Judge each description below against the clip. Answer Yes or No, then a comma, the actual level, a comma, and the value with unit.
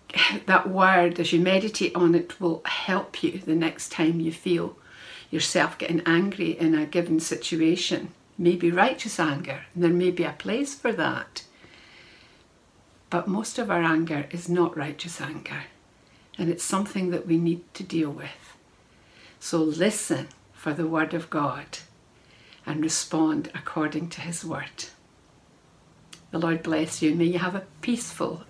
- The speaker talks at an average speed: Yes, average, 155 wpm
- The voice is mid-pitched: Yes, medium, 170 Hz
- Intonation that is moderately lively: No, narrow, 1.9 semitones